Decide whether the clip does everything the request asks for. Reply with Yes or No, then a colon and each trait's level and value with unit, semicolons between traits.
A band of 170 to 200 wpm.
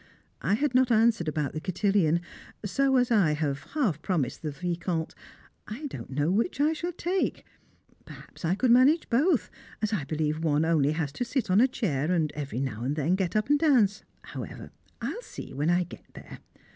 Yes: average, 195 wpm